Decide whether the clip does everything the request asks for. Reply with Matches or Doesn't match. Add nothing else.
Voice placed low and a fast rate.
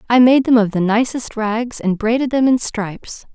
Doesn't match